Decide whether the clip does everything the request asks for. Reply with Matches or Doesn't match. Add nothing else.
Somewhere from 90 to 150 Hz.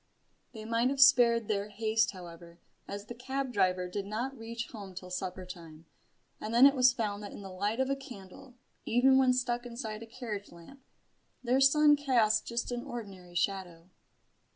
Doesn't match